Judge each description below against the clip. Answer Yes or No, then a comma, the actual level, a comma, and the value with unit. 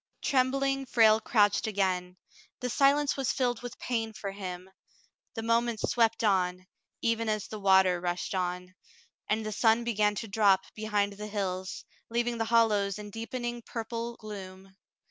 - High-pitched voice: Yes, high, 215 Hz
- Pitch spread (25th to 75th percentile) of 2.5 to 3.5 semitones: Yes, average, 3.2 semitones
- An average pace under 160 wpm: Yes, average, 150 wpm